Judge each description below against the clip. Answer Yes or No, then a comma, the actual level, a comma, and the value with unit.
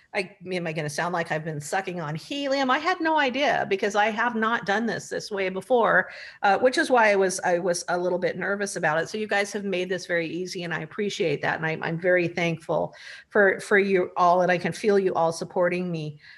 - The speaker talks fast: Yes, fast, 250 wpm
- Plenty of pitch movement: No, average, 3.4 semitones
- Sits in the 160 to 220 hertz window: Yes, medium, 185 Hz